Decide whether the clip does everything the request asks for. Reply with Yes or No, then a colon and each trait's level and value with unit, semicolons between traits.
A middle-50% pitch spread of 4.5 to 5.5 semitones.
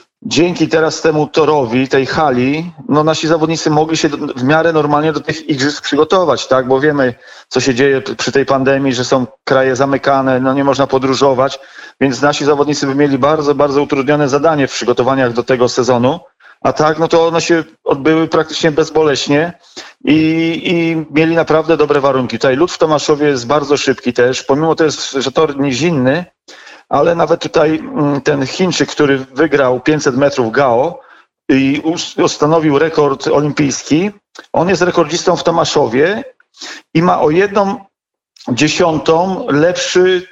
No: average, 3.1 semitones